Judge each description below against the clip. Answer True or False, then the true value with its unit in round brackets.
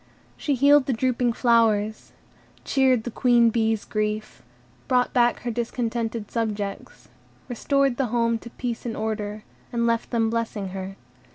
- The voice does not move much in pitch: True (2.0 semitones)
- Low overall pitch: False (230 Hz)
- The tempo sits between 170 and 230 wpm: False (145 wpm)